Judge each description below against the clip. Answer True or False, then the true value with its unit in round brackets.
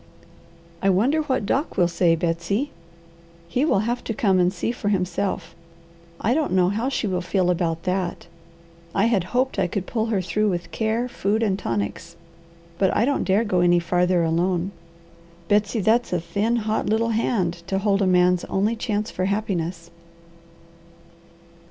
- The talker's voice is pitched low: False (195 Hz)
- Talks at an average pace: True (170 wpm)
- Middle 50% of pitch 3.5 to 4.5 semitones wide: True (3.8 semitones)